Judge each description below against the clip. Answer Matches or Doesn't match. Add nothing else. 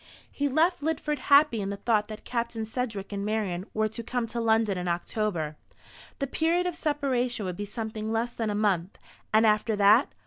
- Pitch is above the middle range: Matches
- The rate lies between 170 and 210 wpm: Matches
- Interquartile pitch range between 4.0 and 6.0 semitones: Doesn't match